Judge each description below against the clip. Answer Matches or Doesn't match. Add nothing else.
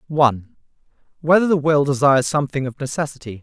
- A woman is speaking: Doesn't match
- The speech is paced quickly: Doesn't match